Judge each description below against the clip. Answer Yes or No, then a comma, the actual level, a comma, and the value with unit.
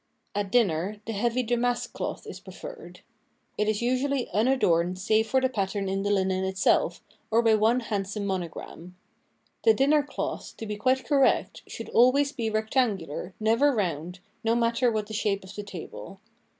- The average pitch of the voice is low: No, high, 215 Hz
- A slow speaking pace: No, average, 180 wpm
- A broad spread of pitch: No, average, 4.1 semitones